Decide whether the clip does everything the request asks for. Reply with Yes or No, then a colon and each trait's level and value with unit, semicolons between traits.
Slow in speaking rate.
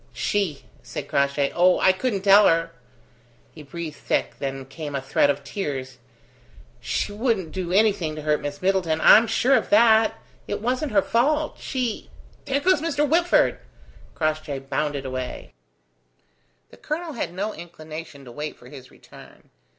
No: average, 155 wpm